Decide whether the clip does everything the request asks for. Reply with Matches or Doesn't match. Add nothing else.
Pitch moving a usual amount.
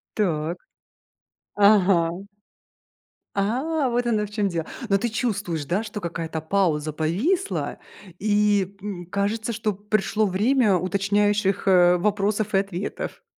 Matches